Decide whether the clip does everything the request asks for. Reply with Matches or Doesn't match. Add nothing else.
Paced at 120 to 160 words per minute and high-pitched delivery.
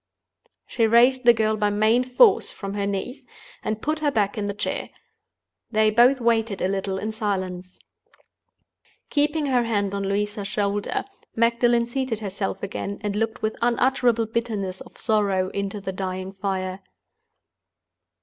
Matches